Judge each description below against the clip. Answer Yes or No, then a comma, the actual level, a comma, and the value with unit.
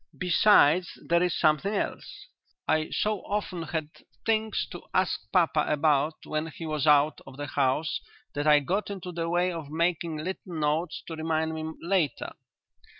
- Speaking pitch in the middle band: Yes, medium, 160 Hz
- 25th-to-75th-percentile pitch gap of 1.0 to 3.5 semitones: Yes, average, 2.9 semitones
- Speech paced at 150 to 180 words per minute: Yes, average, 160 wpm